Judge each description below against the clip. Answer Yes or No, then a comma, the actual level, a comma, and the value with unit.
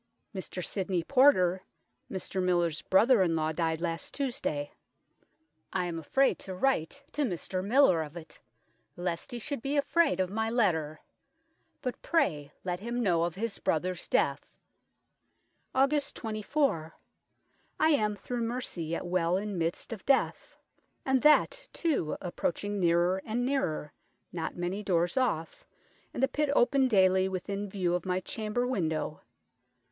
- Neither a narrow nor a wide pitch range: No, wide, 6.2 semitones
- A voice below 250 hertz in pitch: Yes, high, 190 Hz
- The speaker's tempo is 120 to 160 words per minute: Yes, average, 145 wpm